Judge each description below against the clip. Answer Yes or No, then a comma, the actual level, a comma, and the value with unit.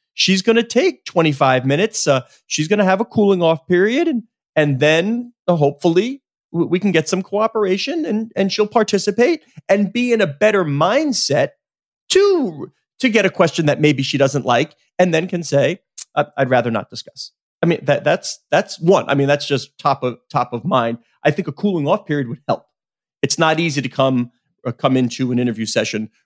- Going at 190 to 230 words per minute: Yes, average, 200 wpm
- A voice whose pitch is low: No, medium, 170 Hz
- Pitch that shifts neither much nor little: No, wide, 6.8 semitones